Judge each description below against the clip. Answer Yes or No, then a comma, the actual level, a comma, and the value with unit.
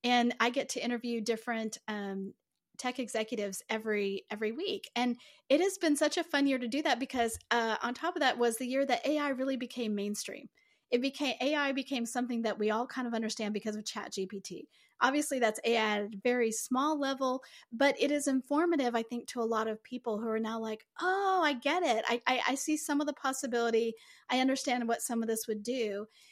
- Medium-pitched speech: No, high, 240 Hz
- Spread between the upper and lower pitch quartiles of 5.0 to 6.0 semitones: No, average, 3.5 semitones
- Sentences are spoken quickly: Yes, fast, 215 wpm